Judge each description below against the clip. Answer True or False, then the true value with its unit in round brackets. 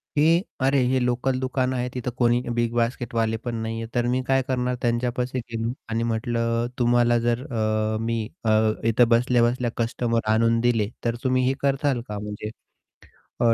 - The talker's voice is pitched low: True (120 Hz)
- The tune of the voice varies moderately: False (1.6 semitones)